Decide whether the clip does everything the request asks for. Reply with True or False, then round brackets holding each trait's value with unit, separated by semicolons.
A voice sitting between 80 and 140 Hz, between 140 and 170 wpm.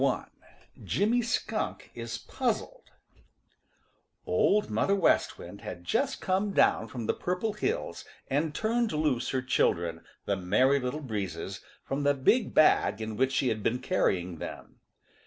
True (135 Hz; 150 wpm)